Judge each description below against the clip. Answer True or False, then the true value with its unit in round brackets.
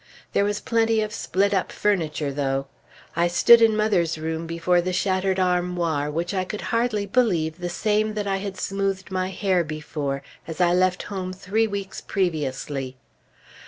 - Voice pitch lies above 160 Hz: True (185 Hz)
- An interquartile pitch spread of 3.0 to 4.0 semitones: True (3.5 semitones)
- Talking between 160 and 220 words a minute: True (165 wpm)